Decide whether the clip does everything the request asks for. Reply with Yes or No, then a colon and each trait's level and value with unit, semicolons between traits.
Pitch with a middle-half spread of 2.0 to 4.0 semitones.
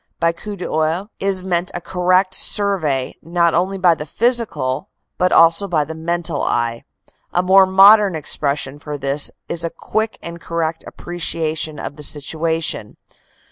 Yes: average, 3.3 semitones